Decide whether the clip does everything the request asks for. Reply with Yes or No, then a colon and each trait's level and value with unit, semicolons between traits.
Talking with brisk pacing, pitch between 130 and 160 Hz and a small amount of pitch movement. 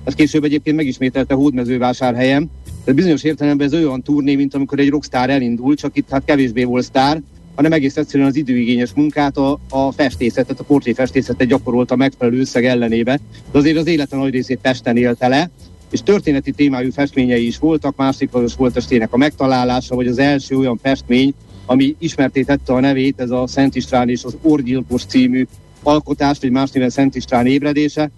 Yes: fast, 180 wpm; low, 135 Hz; narrow, 2.3 semitones